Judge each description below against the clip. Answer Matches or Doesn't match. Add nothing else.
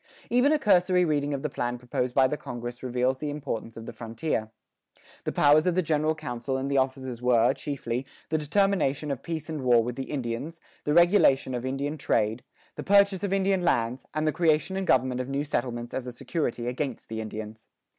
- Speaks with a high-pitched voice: Doesn't match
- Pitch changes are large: Doesn't match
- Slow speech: Doesn't match